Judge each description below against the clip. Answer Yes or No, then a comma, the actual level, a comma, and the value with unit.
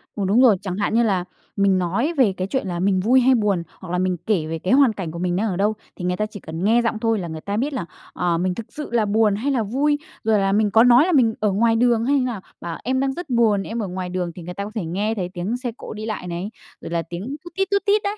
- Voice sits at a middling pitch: No, high, 210 Hz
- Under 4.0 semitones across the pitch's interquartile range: No, average, 4.7 semitones